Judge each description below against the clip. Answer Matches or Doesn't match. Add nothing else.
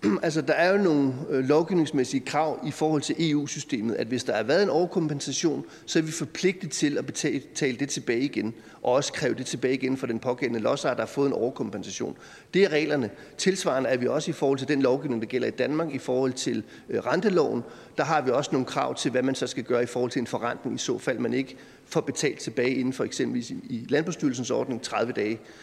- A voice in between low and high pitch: Matches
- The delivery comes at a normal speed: Doesn't match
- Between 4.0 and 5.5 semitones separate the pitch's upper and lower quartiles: Doesn't match